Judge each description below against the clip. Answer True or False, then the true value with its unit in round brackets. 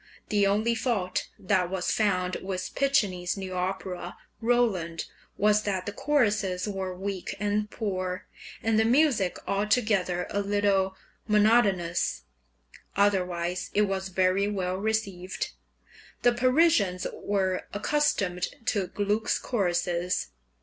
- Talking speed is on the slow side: True (115 wpm)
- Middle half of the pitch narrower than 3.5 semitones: True (2.5 semitones)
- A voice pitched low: False (195 Hz)